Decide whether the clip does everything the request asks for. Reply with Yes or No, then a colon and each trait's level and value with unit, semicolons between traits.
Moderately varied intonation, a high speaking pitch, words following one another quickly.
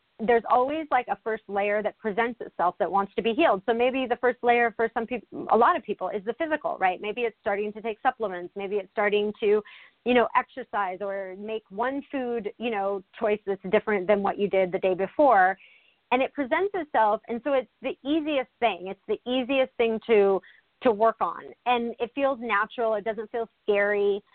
Yes: average, 3.4 semitones; high, 225 Hz; fast, 210 wpm